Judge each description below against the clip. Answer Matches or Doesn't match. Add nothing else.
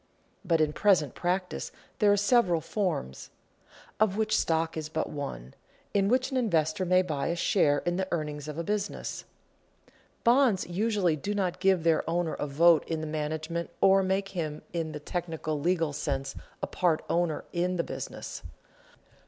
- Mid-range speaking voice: Matches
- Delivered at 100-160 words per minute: Doesn't match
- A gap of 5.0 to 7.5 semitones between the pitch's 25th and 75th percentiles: Doesn't match